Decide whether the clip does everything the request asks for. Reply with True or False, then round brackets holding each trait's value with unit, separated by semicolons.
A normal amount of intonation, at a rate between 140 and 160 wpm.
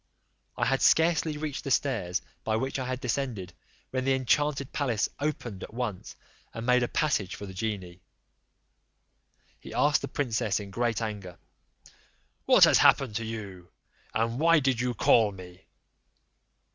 True (4.8 semitones; 155 wpm)